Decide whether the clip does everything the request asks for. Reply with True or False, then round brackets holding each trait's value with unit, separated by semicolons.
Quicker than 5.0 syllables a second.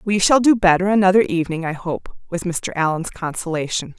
True (5.7 syllables/s)